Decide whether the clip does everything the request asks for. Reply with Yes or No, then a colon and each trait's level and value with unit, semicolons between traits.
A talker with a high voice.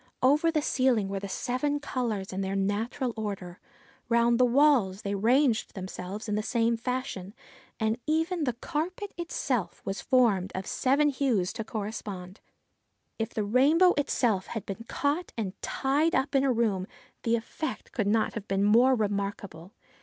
Yes: high, 230 Hz